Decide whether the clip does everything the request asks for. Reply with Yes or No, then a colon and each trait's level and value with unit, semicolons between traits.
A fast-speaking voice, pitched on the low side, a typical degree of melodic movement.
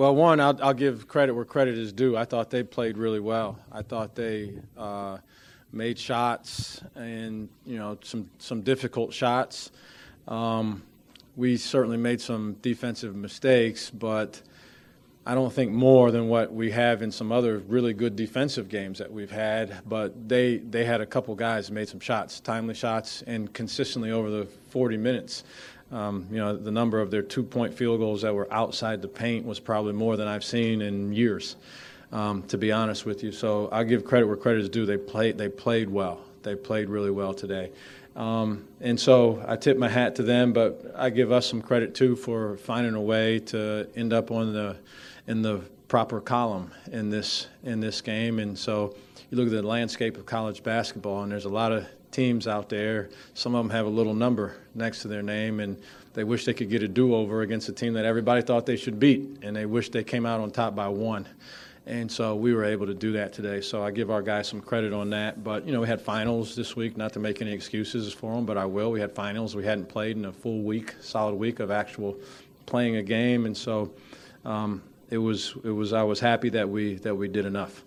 No: fast, 215 wpm; low, 110 Hz; narrow, 2.2 semitones